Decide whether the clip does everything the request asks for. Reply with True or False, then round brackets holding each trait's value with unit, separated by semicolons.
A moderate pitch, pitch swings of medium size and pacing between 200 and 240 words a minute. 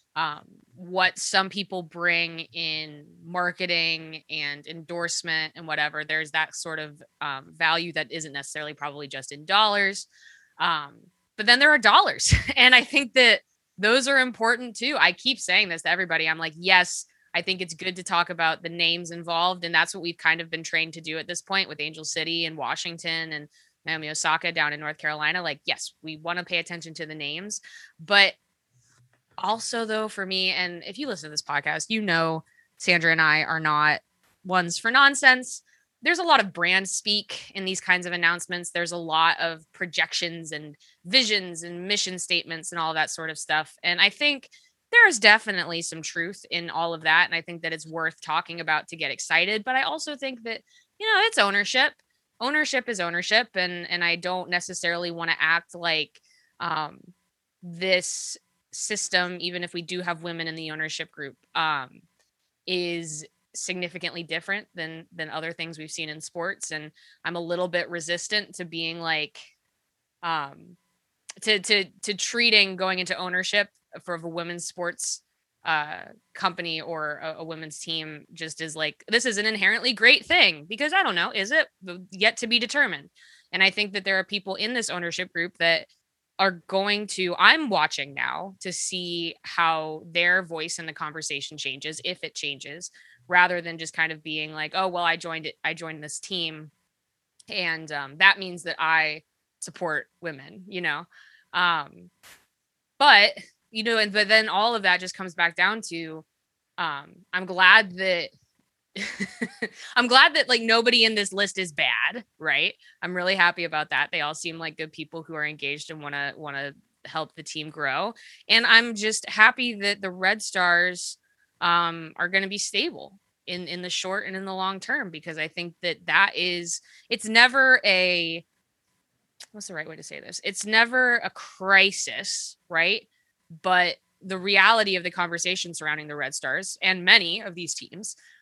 False (175 Hz; 3.4 semitones; 185 wpm)